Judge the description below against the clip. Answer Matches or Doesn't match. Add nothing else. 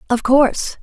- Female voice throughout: Matches